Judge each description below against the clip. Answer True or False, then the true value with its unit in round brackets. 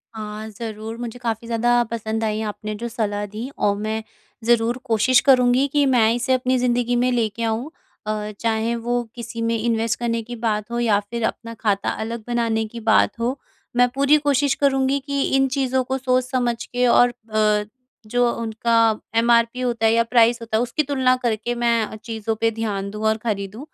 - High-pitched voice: True (230 Hz)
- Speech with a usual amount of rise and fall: False (1.9 semitones)